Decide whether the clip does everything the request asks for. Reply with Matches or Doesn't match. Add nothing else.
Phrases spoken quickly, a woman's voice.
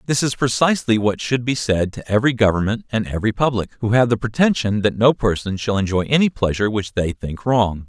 Doesn't match